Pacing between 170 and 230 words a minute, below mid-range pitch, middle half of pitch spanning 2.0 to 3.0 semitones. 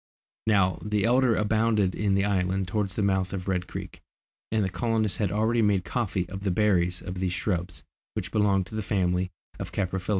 Yes: average, 200 wpm; low, 100 Hz; narrow, 2.6 semitones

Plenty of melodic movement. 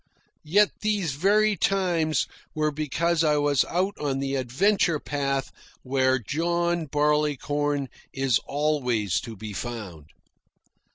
No: average, 4.3 semitones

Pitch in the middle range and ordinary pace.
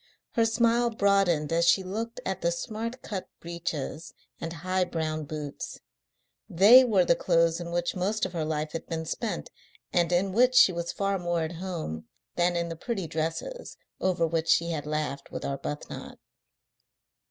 Yes: medium, 175 Hz; average, 170 wpm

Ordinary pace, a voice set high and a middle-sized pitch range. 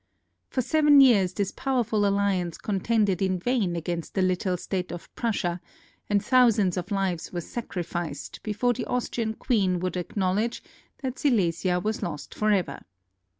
Yes: average, 145 wpm; high, 195 Hz; average, 4.3 semitones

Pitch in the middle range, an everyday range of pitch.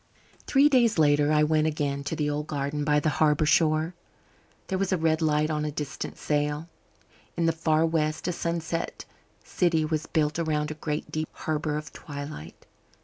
No: medium, 155 Hz; narrow, 1.5 semitones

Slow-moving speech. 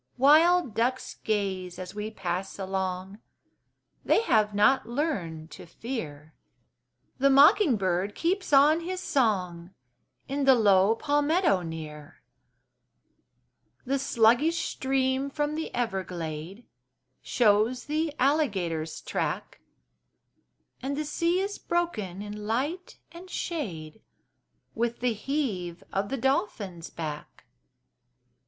Yes: slow, 105 wpm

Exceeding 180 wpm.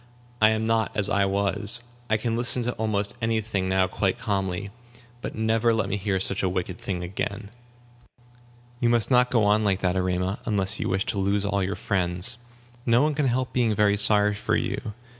Yes: average, 195 wpm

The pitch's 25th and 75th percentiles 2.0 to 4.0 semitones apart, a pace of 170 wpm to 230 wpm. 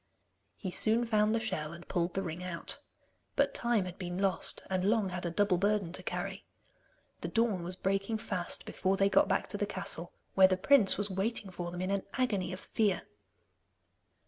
Yes: narrow, 2.6 semitones; average, 200 wpm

